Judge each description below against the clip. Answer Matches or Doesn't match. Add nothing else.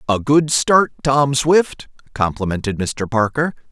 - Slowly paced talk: Matches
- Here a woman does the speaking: Doesn't match